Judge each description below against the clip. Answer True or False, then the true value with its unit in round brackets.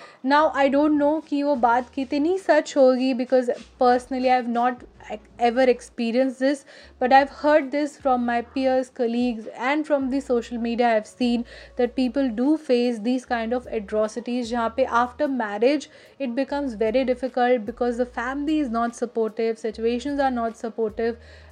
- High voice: True (255 Hz)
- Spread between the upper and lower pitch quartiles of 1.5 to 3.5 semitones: True (2.6 semitones)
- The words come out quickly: False (165 wpm)